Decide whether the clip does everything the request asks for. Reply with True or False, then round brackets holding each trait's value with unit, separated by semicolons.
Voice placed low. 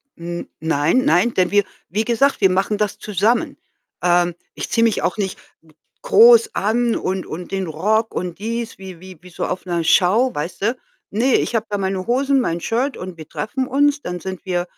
False (200 Hz)